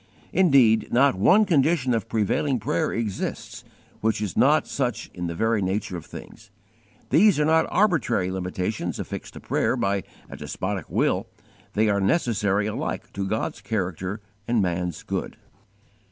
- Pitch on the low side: Yes, low, 105 Hz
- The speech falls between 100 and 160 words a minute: Yes, average, 150 wpm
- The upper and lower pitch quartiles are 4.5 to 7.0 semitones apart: Yes, average, 5.1 semitones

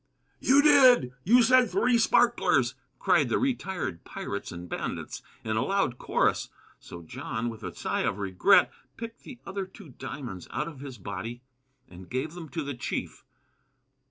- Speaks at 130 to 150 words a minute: No, average, 160 wpm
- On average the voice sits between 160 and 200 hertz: No, medium, 150 Hz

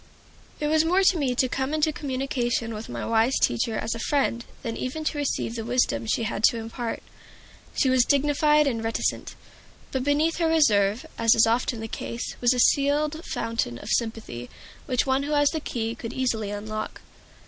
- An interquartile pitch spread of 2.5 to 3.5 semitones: No, average, 4.4 semitones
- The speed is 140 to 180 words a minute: No, average, 190 wpm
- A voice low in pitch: No, very high, 250 Hz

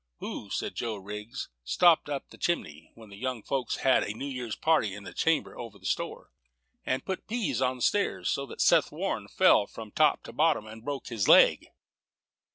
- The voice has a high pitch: No, low, 125 Hz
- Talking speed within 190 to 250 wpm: Yes, average, 200 wpm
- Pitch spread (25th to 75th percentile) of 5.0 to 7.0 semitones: Yes, wide, 5.5 semitones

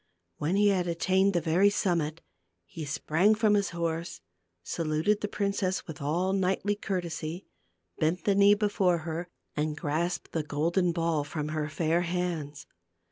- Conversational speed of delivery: Yes, average, 150 wpm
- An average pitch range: Yes, average, 3.6 semitones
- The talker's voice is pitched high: No, medium, 170 Hz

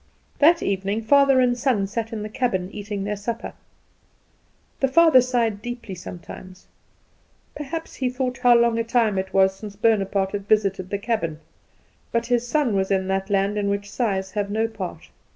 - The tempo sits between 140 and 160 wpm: No, average, 175 wpm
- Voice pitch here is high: Yes, high, 215 Hz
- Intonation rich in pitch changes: No, average, 3.8 semitones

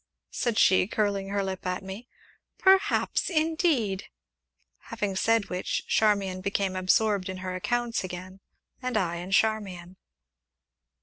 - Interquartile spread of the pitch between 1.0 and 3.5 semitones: Yes, average, 3.2 semitones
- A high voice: Yes, high, 200 Hz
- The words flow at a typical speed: No, slow, 125 wpm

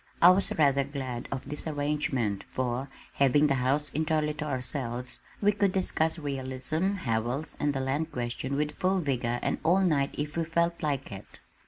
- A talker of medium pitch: Yes, medium, 145 Hz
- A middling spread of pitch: Yes, average, 3.4 semitones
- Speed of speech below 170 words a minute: No, average, 175 wpm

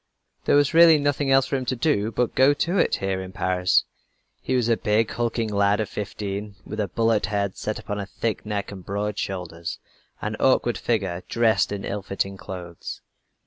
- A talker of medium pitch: No, low, 105 Hz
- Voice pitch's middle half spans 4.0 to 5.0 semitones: No, average, 3.4 semitones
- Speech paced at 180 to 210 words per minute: Yes, average, 200 wpm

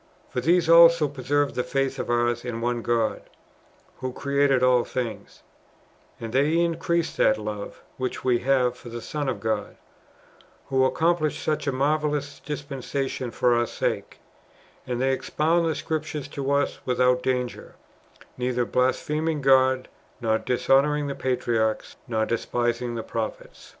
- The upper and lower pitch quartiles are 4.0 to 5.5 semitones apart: No, average, 3.2 semitones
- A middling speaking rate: Yes, average, 145 wpm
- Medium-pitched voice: No, low, 130 Hz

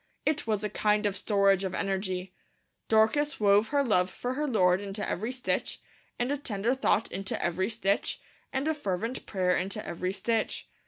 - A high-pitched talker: Yes, high, 210 Hz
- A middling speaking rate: Yes, average, 175 wpm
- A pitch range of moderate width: Yes, average, 4.0 semitones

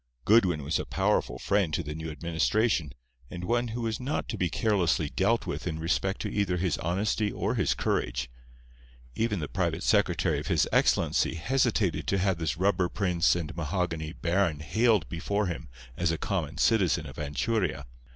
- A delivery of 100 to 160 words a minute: No, average, 175 wpm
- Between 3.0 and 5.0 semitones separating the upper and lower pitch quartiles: Yes, average, 4.4 semitones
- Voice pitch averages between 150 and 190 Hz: No, very low, 90 Hz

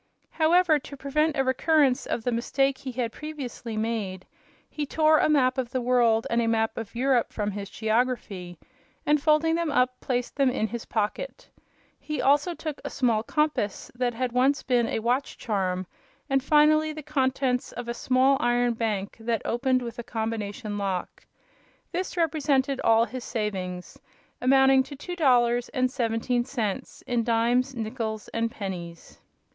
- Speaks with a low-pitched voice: No, very high, 250 Hz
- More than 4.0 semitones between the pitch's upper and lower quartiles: No, average, 3.5 semitones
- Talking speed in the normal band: Yes, average, 165 wpm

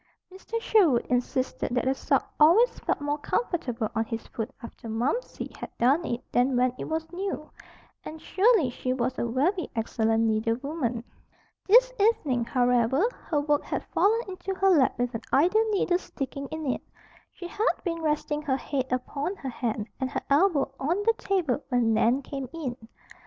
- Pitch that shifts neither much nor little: No, wide, 6.3 semitones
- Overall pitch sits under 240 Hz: No, very high, 280 Hz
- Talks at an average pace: Yes, average, 175 wpm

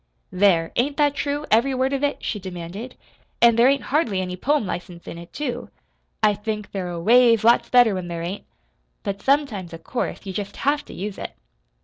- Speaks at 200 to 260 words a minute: Yes, fast, 205 wpm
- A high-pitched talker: Yes, high, 215 Hz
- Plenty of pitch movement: Yes, wide, 6.0 semitones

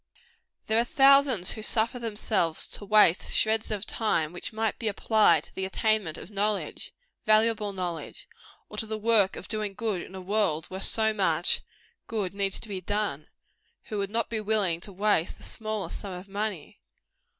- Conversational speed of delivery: Yes, average, 180 wpm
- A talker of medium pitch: No, high, 210 Hz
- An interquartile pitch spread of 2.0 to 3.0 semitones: Yes, narrow, 2.6 semitones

